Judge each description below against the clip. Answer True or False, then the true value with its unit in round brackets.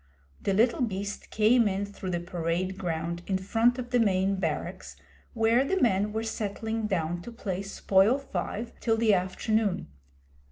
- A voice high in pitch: True (200 Hz)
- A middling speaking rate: True (160 wpm)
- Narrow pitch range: False (3.2 semitones)